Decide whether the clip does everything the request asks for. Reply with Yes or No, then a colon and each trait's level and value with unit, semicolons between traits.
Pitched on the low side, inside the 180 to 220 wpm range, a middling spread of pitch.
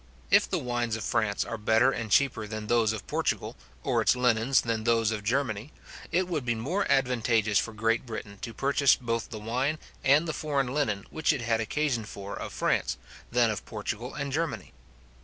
Yes: low, 115 Hz; average, 195 wpm; average, 3.6 semitones